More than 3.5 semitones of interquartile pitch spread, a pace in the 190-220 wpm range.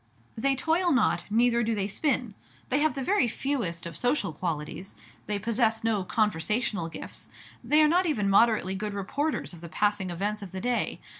No: average, 5.2 semitones; average, 180 wpm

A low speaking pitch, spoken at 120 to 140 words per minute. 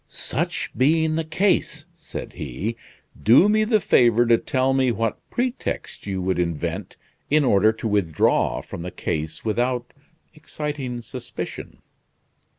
Yes: low, 120 Hz; slow, 135 wpm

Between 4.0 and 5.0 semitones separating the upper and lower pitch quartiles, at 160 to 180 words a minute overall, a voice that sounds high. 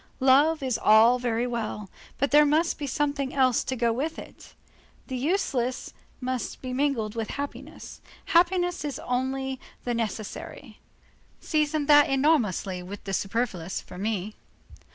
No: average, 4.4 semitones; average, 140 wpm; very high, 255 Hz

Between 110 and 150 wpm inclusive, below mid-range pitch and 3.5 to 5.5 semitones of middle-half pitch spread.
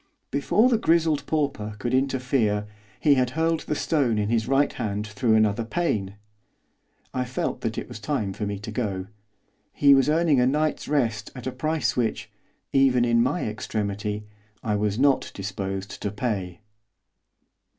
No: average, 160 wpm; low, 120 Hz; average, 5.2 semitones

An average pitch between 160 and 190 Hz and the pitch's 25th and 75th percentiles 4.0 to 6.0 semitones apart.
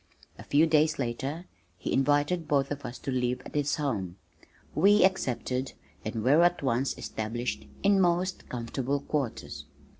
No: medium, 140 Hz; average, 4.4 semitones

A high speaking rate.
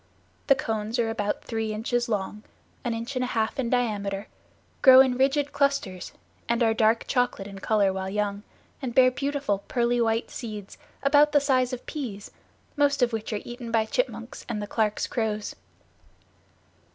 No: average, 170 wpm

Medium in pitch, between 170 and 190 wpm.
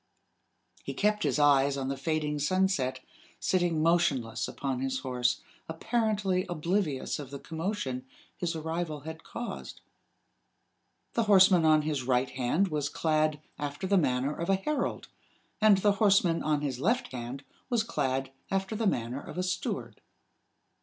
No: medium, 155 Hz; average, 145 wpm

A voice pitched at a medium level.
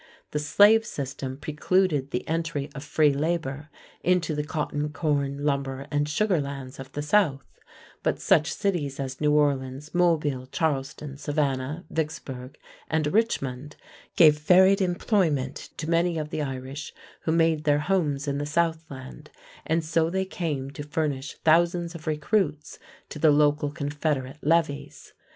Yes: medium, 150 Hz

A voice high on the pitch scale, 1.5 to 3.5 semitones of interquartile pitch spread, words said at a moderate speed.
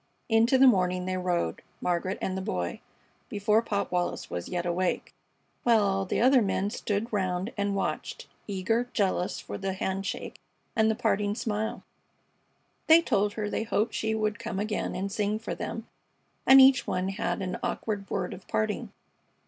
Yes: high, 205 Hz; average, 2.9 semitones; average, 170 wpm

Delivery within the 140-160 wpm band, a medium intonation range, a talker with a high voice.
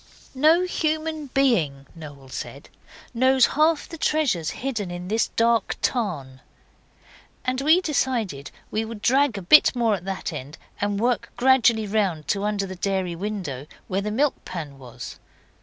No: average, 155 wpm; wide, 7.0 semitones; high, 215 Hz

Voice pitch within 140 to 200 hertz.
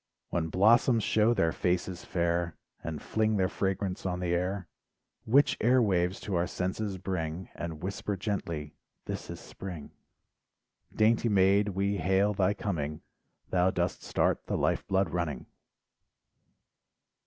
No: very low, 95 Hz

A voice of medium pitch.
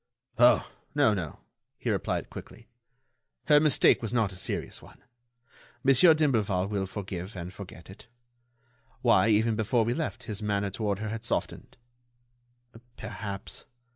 No: low, 110 Hz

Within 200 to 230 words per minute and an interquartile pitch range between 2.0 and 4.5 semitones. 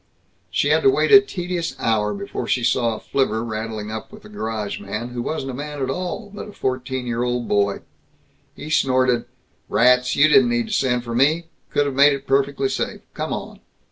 No: fast, 205 wpm; average, 5.2 semitones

